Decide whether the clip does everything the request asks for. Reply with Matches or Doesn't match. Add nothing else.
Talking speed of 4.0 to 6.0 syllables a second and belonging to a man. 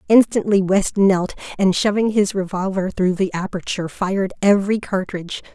Doesn't match